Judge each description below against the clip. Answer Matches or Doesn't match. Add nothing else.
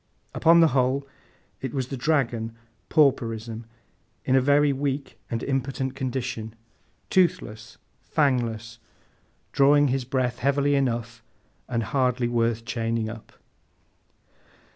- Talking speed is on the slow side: Matches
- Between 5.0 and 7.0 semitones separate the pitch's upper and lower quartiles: Doesn't match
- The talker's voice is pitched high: Doesn't match